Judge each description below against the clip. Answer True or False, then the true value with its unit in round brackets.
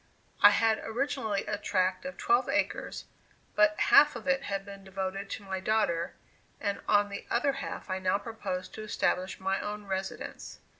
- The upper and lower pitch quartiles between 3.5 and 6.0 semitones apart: False (2.5 semitones)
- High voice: True (205 Hz)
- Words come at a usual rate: True (170 wpm)